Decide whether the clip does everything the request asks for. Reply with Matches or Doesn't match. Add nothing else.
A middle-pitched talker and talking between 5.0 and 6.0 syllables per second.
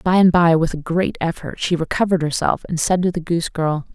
Matches